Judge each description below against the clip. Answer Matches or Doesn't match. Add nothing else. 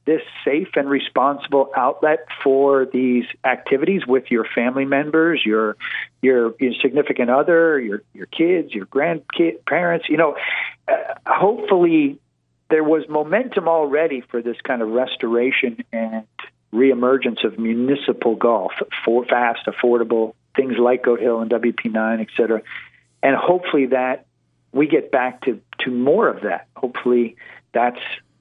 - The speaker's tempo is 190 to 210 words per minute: Doesn't match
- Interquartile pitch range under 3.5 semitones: Doesn't match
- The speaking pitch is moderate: Doesn't match